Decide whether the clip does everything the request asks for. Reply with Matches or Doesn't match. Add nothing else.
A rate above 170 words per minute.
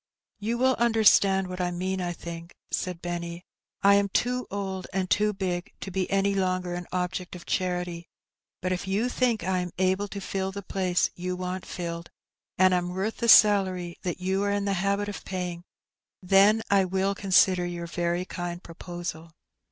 Matches